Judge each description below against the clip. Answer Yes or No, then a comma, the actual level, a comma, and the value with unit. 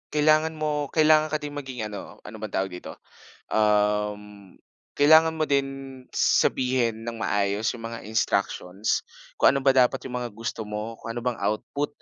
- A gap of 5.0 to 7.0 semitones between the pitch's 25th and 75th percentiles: Yes, wide, 5.4 semitones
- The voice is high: No, low, 120 Hz